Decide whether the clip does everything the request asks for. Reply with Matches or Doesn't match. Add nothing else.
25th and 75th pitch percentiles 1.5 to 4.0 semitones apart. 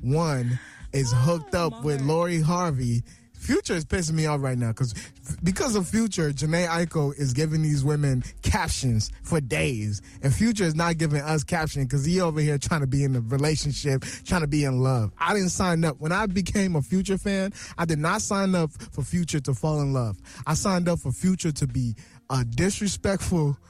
Doesn't match